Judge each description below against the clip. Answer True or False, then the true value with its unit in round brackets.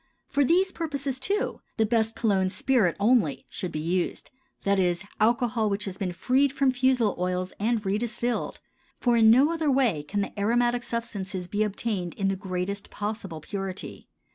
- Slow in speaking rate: False (165 wpm)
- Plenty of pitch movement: False (4.3 semitones)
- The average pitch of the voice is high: True (215 Hz)